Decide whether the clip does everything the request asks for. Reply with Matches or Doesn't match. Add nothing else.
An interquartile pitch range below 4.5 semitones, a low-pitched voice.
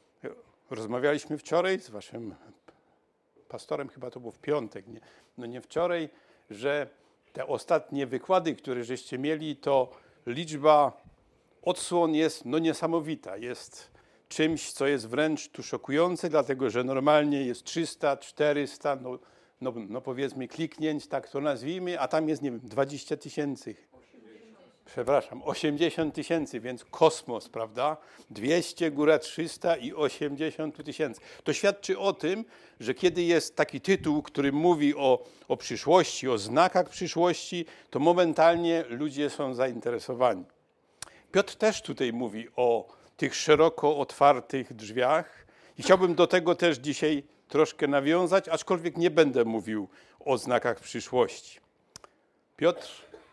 Doesn't match